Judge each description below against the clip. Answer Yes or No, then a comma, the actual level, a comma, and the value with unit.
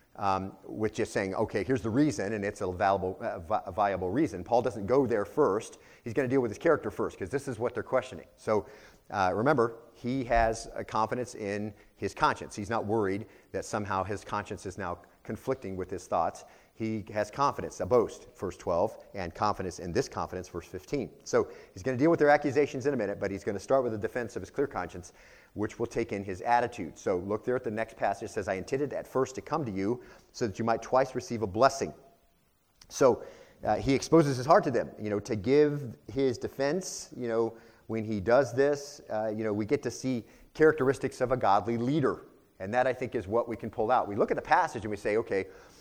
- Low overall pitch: Yes, low, 115 Hz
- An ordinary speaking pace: No, fast, 230 wpm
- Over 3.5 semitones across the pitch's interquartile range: Yes, average, 4.2 semitones